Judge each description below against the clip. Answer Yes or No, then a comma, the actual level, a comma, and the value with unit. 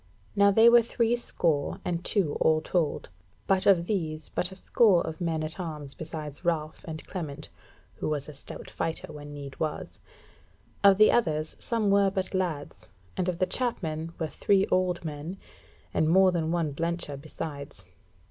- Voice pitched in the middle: Yes, medium, 165 Hz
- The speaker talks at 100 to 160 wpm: No, average, 170 wpm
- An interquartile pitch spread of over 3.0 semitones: Yes, average, 3.5 semitones